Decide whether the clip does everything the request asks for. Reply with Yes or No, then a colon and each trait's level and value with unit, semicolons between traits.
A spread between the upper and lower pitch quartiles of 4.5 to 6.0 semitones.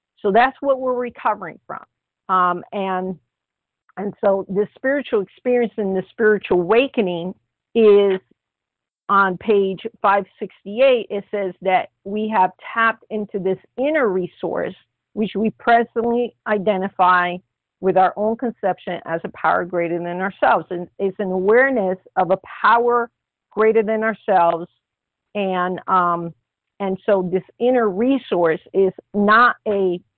No: average, 3.3 semitones